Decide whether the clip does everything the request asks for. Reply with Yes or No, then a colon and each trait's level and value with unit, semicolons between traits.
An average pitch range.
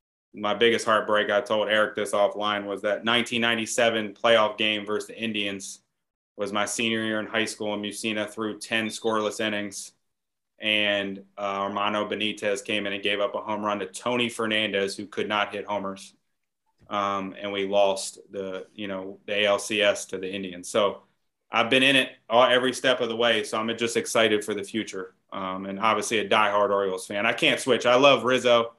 No: narrow, 1.9 semitones